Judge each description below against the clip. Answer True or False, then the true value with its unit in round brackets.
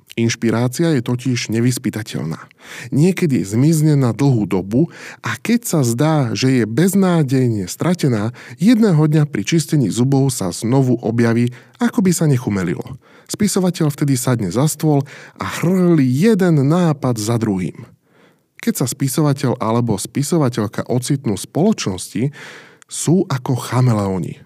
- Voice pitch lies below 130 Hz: False (135 Hz)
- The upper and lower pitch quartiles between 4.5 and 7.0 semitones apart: True (5.2 semitones)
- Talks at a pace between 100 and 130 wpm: True (125 wpm)